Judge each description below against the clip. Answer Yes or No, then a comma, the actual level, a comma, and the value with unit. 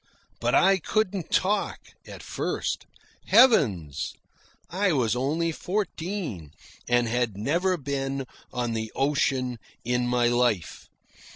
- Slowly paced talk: Yes, slow, 110 wpm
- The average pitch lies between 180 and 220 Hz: No, low, 135 Hz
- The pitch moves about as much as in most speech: No, wide, 6.8 semitones